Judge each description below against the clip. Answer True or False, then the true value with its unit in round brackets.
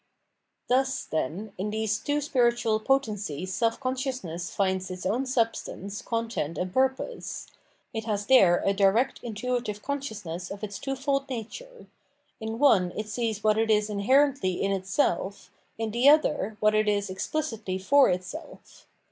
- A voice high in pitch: True (220 Hz)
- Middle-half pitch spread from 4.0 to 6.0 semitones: True (4.7 semitones)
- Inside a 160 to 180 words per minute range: False (150 wpm)